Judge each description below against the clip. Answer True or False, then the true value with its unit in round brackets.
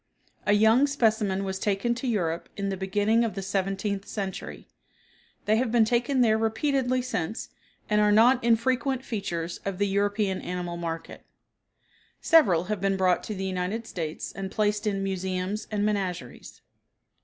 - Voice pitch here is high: True (205 Hz)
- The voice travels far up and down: False (3.0 semitones)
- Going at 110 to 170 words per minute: True (155 wpm)